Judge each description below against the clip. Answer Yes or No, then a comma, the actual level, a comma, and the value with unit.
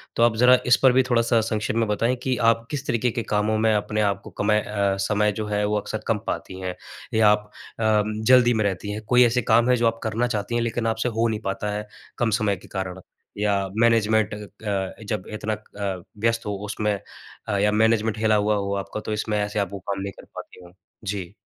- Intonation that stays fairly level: Yes, narrow, 1.9 semitones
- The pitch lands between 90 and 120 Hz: Yes, low, 105 Hz